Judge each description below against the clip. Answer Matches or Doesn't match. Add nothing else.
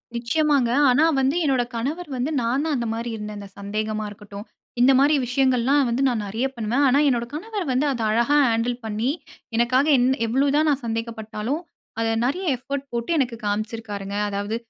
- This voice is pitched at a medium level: Doesn't match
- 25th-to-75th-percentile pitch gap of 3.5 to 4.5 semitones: Matches